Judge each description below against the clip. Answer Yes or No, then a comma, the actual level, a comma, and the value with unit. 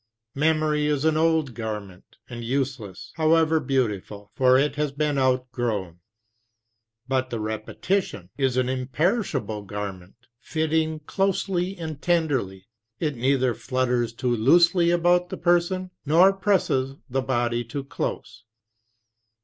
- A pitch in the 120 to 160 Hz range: Yes, low, 135 Hz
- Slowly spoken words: Yes, slow, 120 wpm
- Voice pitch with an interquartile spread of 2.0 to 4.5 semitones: No, average, 5.1 semitones